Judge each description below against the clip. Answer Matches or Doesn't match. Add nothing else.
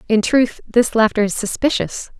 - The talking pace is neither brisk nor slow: Matches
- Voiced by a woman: Matches